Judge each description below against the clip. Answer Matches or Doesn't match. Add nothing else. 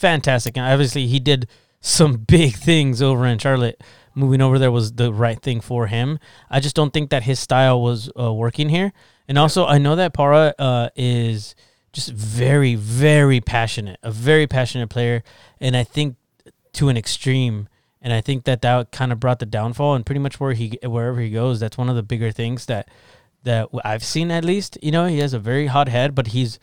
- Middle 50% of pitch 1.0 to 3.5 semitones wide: Matches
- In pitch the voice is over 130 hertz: Doesn't match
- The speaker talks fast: Matches